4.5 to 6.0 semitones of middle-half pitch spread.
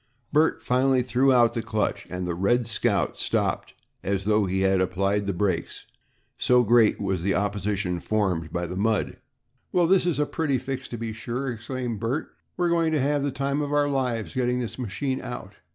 Yes: average, 5.1 semitones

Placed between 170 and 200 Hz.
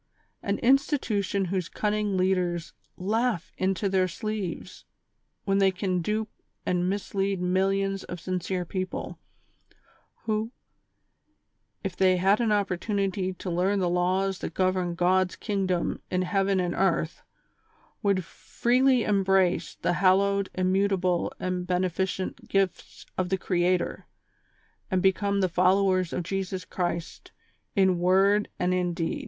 Yes: high, 190 Hz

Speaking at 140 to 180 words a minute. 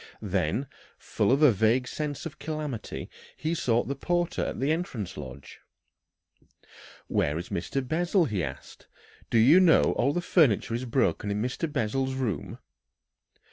Yes: average, 155 wpm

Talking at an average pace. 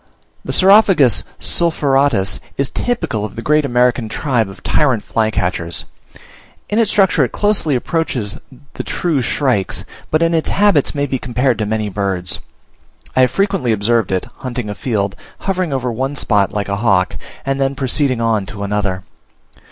Yes: average, 160 wpm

